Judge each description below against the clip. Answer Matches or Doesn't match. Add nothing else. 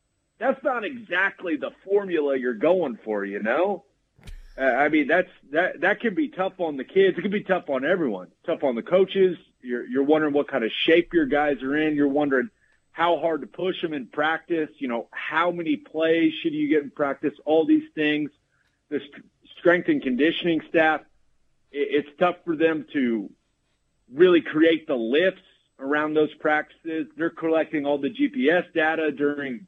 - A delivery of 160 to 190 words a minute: Matches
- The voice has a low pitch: Doesn't match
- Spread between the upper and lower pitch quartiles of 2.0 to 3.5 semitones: Doesn't match